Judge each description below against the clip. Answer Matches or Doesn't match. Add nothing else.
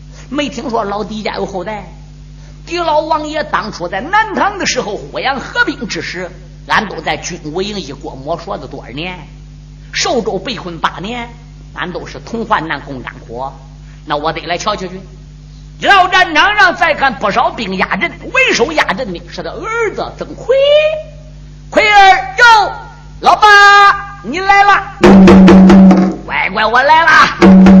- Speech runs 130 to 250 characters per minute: Matches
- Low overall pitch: Doesn't match